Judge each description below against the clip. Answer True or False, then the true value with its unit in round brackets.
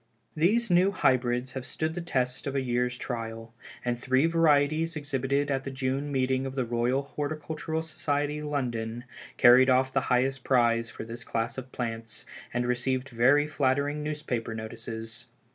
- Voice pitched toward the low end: True (130 Hz)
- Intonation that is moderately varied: True (3.2 semitones)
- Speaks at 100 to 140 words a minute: False (160 wpm)